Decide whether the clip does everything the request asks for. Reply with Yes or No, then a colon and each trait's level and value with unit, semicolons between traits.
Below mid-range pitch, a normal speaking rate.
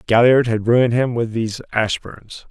Yes: low, 115 Hz; average, 170 wpm